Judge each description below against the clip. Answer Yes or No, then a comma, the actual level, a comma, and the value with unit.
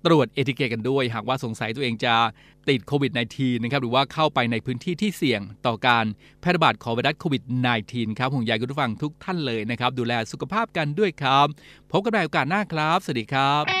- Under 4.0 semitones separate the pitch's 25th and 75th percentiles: No, average, 4.3 semitones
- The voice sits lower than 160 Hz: Yes, low, 135 Hz